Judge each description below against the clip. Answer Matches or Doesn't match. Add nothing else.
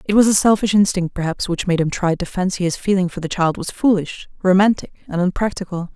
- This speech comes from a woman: Matches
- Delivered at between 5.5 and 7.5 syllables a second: Matches